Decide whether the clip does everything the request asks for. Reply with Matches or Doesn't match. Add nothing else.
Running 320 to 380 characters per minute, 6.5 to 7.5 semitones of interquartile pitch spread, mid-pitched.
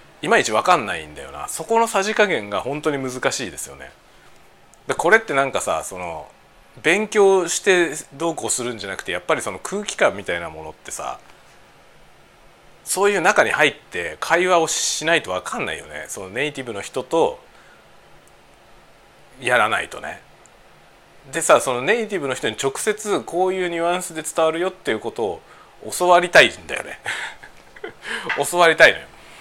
Matches